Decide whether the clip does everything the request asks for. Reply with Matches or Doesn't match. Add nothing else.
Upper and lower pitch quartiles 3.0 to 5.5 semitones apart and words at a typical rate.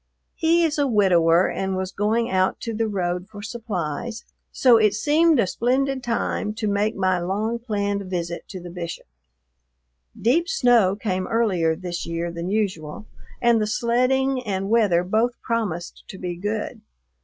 Matches